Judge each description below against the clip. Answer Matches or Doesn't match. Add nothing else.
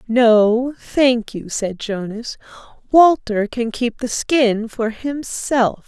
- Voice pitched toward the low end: Doesn't match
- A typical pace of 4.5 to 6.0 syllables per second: Doesn't match